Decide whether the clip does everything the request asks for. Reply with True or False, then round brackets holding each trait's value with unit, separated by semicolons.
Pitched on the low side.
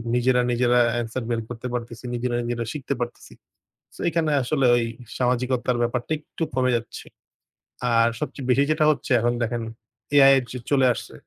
True (125 Hz)